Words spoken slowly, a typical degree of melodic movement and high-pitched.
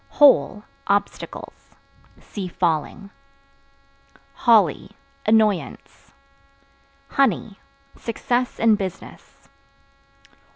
Yes: slow, 55 wpm; average, 3.4 semitones; high, 210 Hz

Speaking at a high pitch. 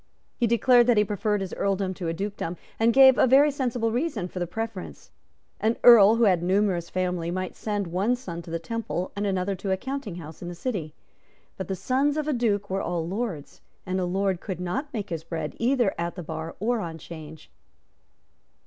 Yes: high, 195 Hz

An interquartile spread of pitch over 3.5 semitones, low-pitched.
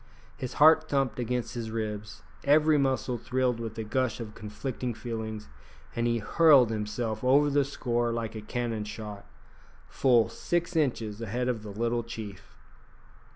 No: average, 3.1 semitones; low, 120 Hz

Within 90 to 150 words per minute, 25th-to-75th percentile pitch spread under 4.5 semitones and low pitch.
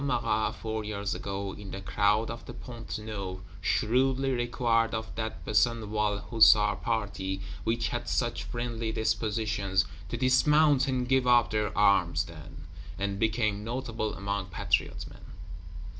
Yes: average, 140 wpm; average, 2.7 semitones; low, 110 Hz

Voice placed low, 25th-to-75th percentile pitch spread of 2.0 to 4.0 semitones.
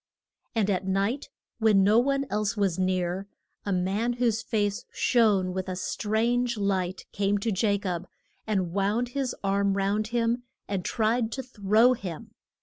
No: high, 205 Hz; average, 3.2 semitones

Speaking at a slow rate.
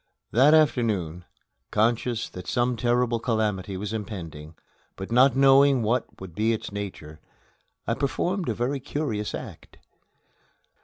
Yes: slow, 125 wpm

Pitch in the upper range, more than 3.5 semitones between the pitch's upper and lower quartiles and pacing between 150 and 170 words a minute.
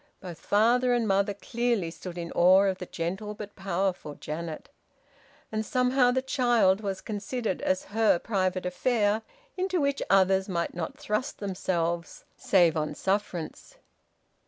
No: high, 195 Hz; average, 4.3 semitones; average, 140 wpm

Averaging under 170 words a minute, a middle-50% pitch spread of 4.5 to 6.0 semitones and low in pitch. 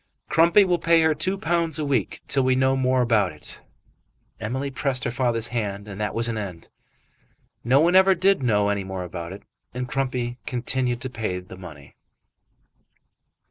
No: average, 180 wpm; average, 5.3 semitones; low, 125 Hz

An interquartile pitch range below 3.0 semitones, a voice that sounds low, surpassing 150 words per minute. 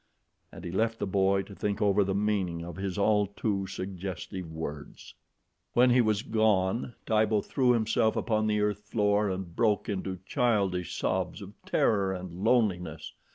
Yes: narrow, 2.5 semitones; low, 100 Hz; average, 160 wpm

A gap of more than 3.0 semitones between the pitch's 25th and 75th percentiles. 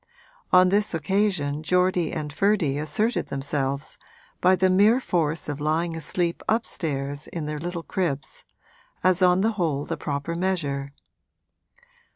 Yes: average, 4.1 semitones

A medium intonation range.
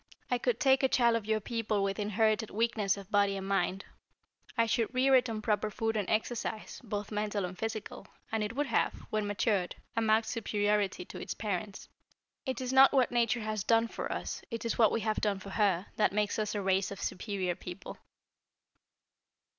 No: narrow, 2.3 semitones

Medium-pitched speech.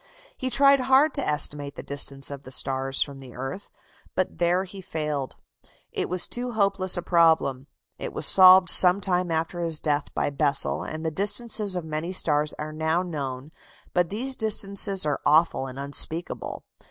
Yes: medium, 165 Hz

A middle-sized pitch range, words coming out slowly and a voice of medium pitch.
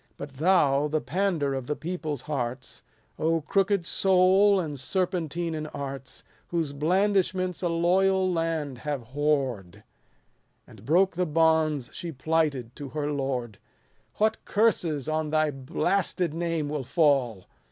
Yes: average, 4.2 semitones; slow, 130 wpm; medium, 155 Hz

